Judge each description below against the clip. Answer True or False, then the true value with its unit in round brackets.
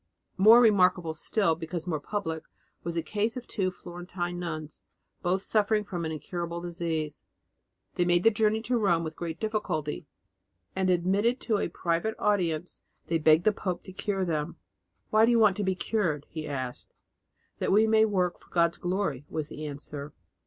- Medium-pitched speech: True (175 Hz)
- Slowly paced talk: False (175 wpm)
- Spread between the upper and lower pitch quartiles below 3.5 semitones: False (4.2 semitones)